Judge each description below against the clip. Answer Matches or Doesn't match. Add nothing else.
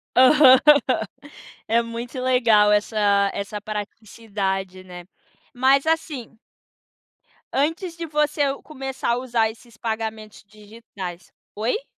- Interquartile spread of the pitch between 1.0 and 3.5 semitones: Doesn't match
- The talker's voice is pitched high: Matches